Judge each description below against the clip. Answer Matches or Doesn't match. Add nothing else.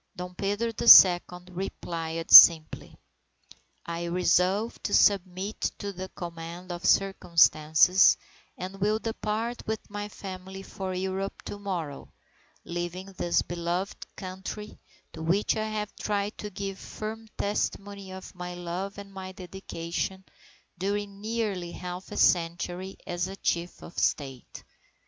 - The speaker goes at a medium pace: Doesn't match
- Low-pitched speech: Doesn't match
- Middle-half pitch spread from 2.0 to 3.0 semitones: Matches